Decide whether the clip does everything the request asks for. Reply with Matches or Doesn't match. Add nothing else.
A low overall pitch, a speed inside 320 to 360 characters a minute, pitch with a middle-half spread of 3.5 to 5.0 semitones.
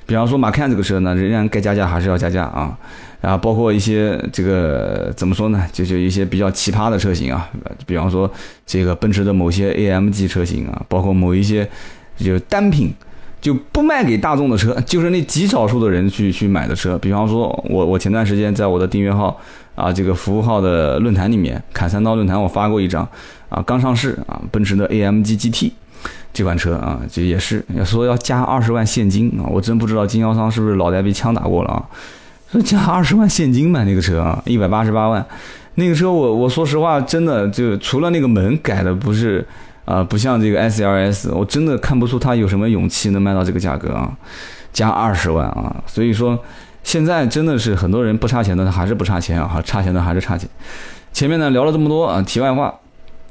Matches